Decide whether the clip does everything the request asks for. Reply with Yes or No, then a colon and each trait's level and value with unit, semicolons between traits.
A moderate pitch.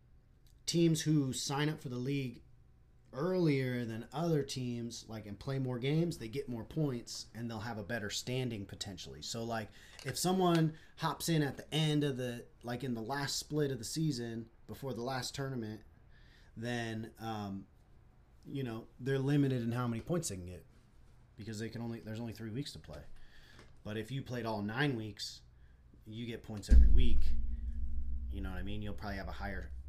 No: low, 115 Hz